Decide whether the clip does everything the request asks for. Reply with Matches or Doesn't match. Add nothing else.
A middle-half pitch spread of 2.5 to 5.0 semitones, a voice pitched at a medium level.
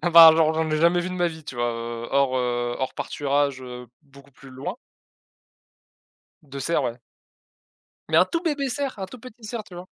Doesn't match